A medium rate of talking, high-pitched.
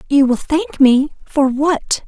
Yes: average, 145 wpm; very high, 285 Hz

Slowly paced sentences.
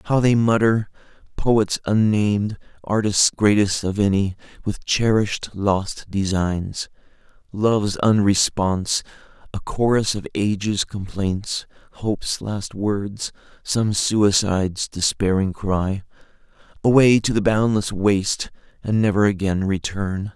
Yes: slow, 95 wpm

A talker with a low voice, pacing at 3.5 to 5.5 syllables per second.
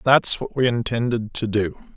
Yes: low, 115 Hz; 4.7 syllables/s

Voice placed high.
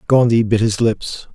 No: low, 110 Hz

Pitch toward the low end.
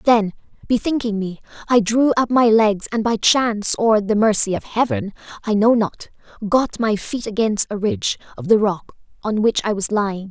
No: high, 215 Hz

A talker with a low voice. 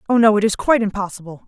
No: high, 210 Hz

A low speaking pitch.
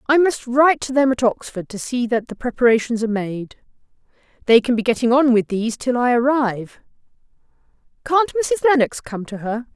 No: high, 245 Hz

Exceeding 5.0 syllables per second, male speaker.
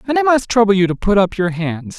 Yes: 6.0 syllables/s; male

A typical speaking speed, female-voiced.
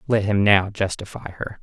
No: average, 185 wpm; male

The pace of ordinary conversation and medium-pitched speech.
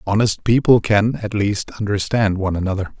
No: average, 160 wpm; low, 105 Hz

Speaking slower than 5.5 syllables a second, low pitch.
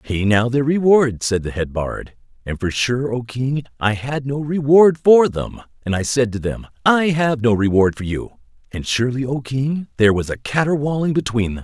Yes: 4.9 syllables/s; low, 125 Hz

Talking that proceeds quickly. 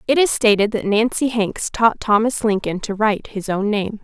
Yes: fast, 210 wpm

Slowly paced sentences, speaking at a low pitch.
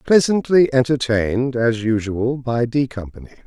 Yes: slow, 120 wpm; low, 125 Hz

